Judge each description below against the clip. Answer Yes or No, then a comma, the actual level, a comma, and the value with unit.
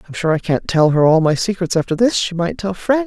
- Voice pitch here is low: No, medium, 180 Hz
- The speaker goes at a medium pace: No, fast, 295 wpm